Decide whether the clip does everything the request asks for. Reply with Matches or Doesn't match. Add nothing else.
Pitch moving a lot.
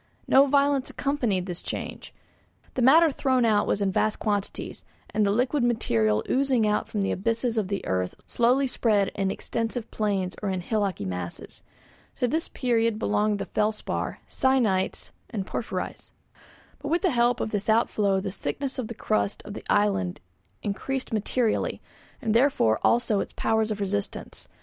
Doesn't match